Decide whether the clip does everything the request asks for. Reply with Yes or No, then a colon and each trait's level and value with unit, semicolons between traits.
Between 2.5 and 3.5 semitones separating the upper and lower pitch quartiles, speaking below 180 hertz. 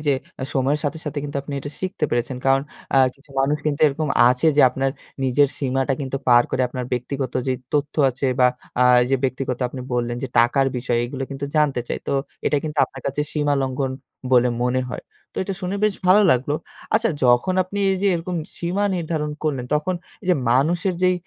Yes: average, 3.2 semitones; medium, 140 Hz